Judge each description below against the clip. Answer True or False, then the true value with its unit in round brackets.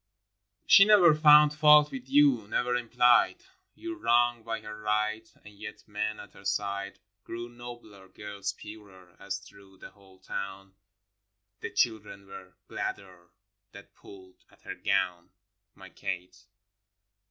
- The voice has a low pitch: True (105 Hz)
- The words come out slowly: False (145 wpm)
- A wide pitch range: False (3.7 semitones)